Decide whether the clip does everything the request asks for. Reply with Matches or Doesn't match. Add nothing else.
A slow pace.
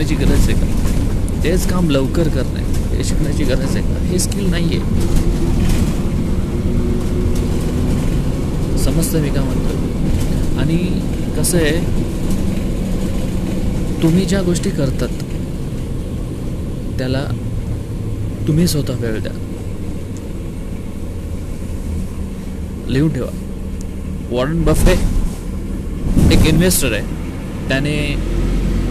Matches